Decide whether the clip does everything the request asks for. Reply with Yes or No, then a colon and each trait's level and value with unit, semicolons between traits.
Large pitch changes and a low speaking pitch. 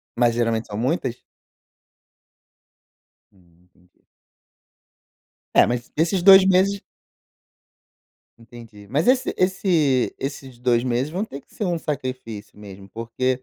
Yes: wide, 6.3 semitones; low, 125 Hz